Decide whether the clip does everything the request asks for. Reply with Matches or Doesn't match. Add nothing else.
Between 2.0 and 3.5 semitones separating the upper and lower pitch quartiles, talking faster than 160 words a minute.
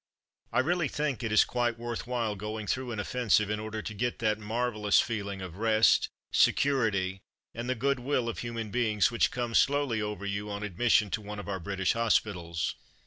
Matches